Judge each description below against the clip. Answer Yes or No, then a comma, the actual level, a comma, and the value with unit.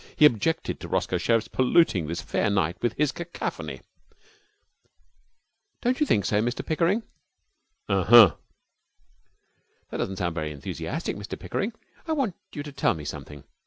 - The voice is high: No, low, 115 Hz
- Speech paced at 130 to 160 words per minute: Yes, average, 150 wpm